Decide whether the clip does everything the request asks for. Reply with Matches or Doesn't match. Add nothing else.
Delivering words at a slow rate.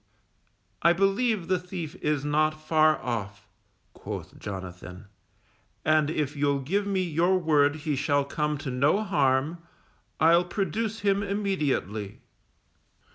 Matches